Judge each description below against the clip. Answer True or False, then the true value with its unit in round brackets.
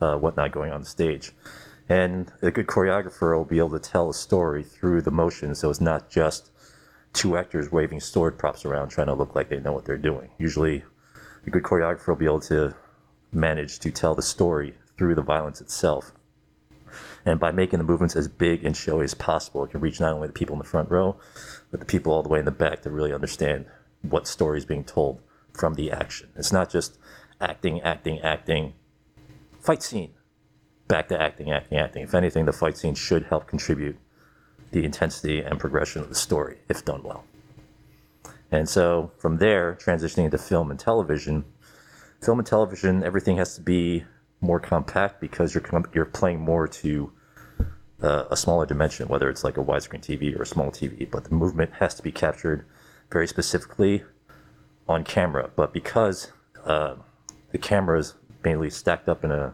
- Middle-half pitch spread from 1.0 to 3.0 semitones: True (2.7 semitones)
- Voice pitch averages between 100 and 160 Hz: False (80 Hz)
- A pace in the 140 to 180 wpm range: False (195 wpm)